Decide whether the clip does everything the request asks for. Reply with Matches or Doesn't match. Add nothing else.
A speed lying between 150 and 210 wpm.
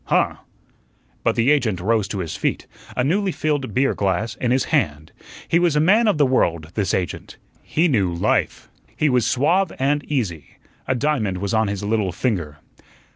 Matches